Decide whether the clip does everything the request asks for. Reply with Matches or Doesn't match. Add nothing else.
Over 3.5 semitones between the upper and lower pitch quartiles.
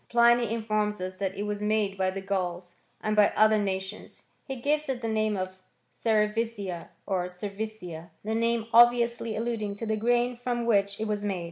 Doesn't match